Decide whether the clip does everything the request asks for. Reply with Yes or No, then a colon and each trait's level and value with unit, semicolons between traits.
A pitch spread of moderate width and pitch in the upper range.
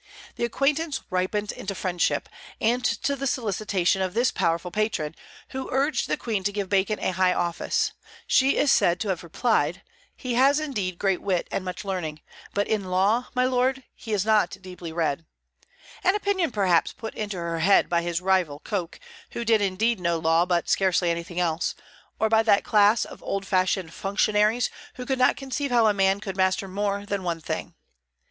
Yes: average, 4.3 semitones; high, 200 Hz